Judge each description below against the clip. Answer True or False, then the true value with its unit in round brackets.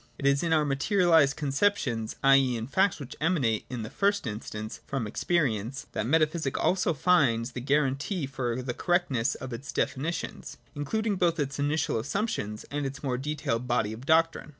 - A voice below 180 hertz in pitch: True (140 Hz)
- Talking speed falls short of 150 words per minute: False (175 wpm)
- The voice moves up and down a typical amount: True (5.0 semitones)